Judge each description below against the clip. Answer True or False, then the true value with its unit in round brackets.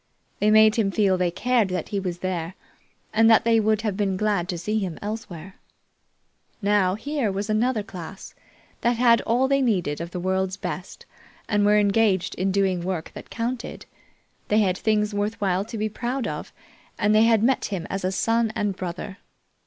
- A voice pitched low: False (205 Hz)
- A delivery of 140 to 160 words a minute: False (190 wpm)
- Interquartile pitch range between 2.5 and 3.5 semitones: True (3.0 semitones)